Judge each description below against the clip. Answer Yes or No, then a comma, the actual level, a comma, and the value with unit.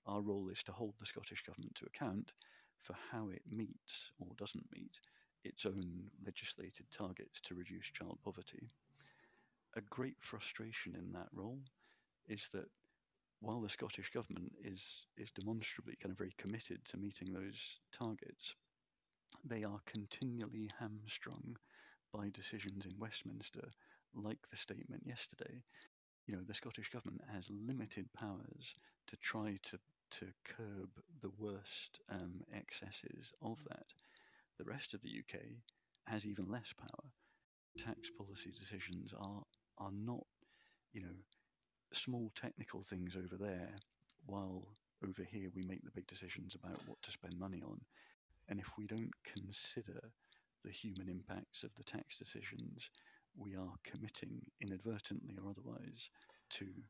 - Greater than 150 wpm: No, average, 140 wpm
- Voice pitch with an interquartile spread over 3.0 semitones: No, narrow, 2.4 semitones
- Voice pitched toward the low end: Yes, low, 100 Hz